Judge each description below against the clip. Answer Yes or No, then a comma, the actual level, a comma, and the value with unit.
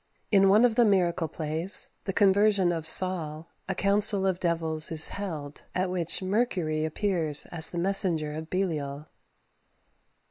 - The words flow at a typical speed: Yes, average, 145 wpm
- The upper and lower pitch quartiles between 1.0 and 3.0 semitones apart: No, average, 3.7 semitones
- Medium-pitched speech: Yes, medium, 175 Hz